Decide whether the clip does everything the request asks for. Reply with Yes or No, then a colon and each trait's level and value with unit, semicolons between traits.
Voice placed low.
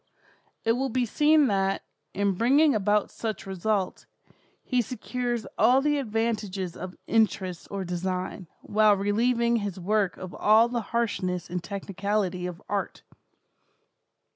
No: high, 210 Hz